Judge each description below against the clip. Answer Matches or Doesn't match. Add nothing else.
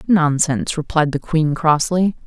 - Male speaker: Doesn't match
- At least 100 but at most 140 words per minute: Matches